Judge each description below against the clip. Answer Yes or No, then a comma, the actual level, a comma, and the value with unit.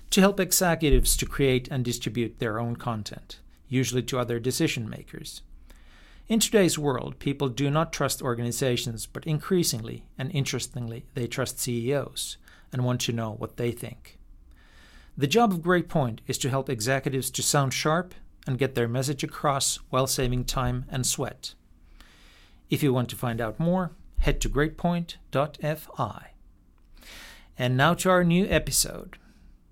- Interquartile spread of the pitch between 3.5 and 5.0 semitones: Yes, average, 4.1 semitones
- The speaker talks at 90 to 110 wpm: No, average, 150 wpm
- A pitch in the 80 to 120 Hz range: No, low, 130 Hz